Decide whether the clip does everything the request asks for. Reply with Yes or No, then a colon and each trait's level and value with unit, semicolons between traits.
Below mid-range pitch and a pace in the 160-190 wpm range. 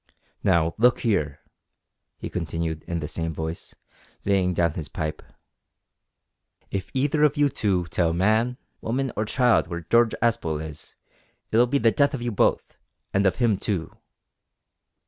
No: very low, 95 Hz; average, 150 wpm